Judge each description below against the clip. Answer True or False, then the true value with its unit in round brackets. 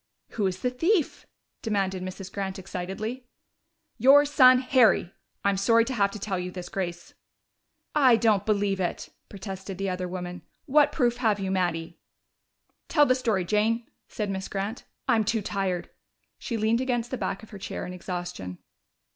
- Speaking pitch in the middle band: False (200 Hz)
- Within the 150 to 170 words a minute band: True (165 wpm)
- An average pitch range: True (4.1 semitones)